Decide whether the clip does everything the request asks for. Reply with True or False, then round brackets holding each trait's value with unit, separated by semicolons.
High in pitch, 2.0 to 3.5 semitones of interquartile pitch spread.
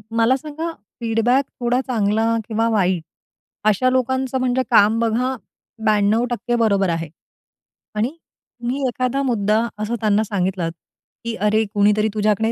True (225 Hz; 3.1 semitones)